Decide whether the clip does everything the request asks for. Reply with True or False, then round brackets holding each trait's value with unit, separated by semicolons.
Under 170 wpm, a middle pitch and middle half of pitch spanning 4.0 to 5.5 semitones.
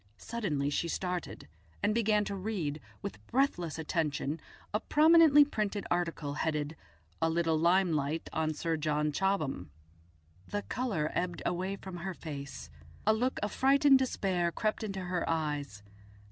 True (140 wpm; 175 Hz; 5.2 semitones)